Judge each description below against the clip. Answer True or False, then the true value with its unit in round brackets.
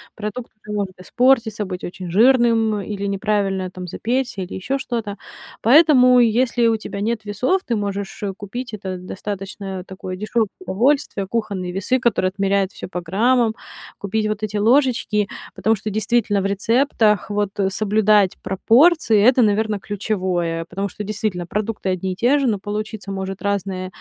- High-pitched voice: True (210 Hz)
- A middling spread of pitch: True (3.1 semitones)